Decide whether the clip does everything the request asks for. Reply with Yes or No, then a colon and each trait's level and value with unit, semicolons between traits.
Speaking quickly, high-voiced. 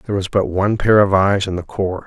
No: fast, 290 wpm; low, 100 Hz